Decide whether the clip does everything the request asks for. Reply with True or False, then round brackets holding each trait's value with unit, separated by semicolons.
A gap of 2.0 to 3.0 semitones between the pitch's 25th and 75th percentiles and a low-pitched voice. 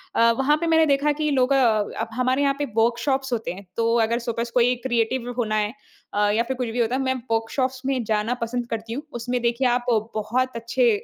False (2.6 semitones; 245 Hz)